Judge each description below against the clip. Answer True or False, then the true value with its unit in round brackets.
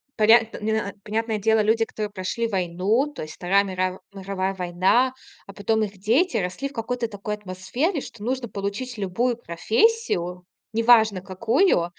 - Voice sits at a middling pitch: False (210 Hz)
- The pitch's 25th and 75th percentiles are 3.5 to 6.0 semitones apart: True (3.8 semitones)